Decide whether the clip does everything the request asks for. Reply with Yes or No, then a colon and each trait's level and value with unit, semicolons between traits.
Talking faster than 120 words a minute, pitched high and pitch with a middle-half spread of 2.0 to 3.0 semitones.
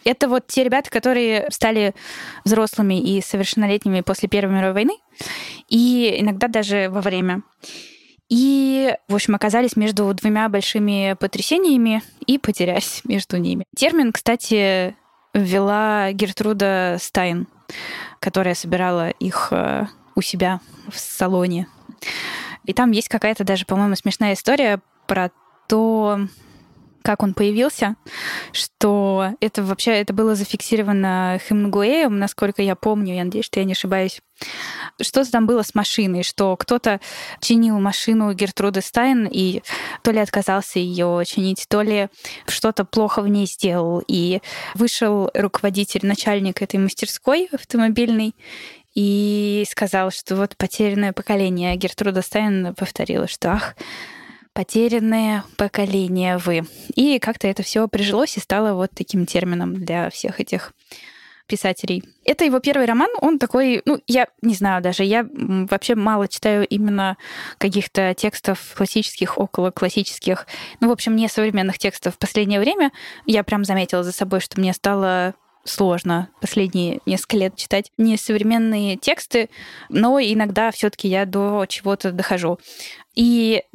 Yes: average, 130 wpm; high, 205 Hz; average, 2.7 semitones